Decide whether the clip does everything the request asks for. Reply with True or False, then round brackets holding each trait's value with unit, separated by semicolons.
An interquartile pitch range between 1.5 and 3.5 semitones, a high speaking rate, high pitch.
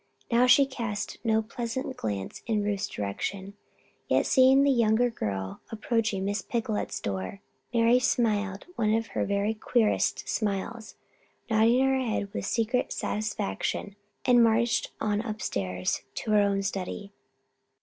False (2.9 semitones; 135 wpm; 215 Hz)